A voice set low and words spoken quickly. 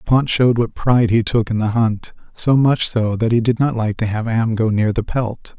Yes: low, 115 Hz; fast, 260 wpm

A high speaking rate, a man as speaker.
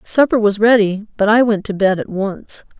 No: fast, 215 wpm; female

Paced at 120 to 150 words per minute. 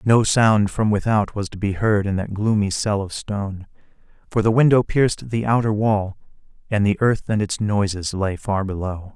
No: average, 195 wpm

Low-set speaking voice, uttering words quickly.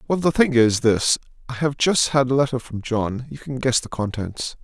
Yes: low, 130 Hz; fast, 235 wpm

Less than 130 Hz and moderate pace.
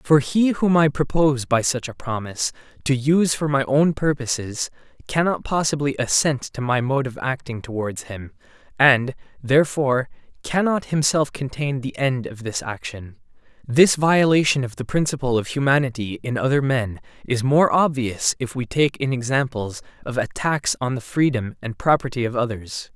No: low, 135 Hz; average, 160 wpm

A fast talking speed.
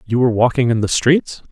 Yes: fast, 240 wpm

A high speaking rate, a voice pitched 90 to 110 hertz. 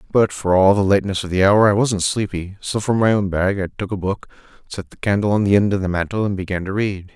Yes: fast, 275 wpm; low, 100 Hz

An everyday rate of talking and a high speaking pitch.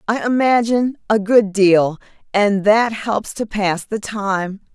Yes: average, 150 wpm; high, 210 Hz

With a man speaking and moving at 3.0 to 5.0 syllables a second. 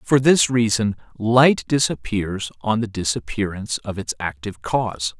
Yes: male; 4.6 syllables/s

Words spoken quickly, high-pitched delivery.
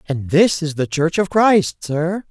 No: fast, 210 wpm; medium, 165 Hz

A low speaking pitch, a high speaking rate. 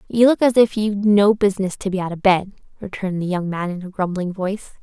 No: high, 195 Hz; fast, 250 wpm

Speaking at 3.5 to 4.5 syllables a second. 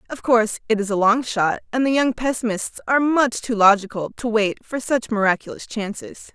No: 5.4 syllables/s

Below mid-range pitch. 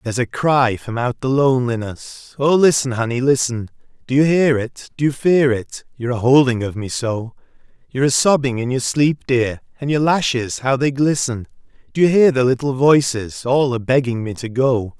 Yes: low, 130 Hz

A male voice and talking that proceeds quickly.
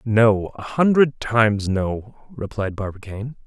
No: male; slow, 120 wpm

